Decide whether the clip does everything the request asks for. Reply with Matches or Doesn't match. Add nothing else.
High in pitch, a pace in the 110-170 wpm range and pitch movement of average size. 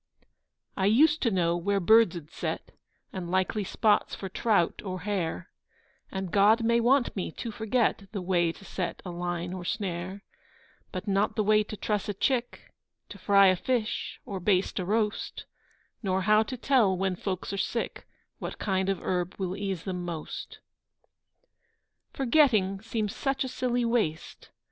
Matches